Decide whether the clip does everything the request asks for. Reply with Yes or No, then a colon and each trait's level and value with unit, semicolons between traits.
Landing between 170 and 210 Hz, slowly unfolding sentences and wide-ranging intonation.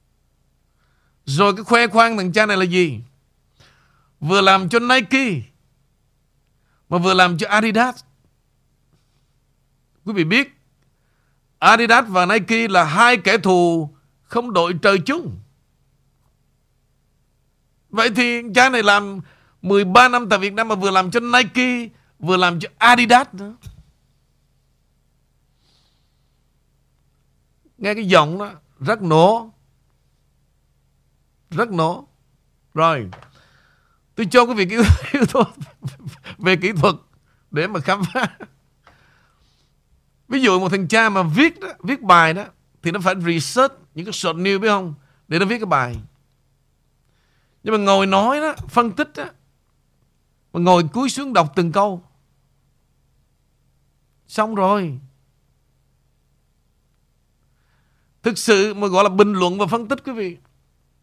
Yes: high, 190 Hz; slow, 125 wpm; wide, 6.5 semitones